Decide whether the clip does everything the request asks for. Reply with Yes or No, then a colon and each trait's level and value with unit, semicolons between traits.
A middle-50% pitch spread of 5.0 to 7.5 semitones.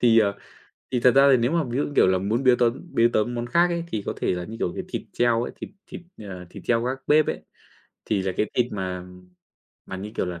No: average, 4.1 semitones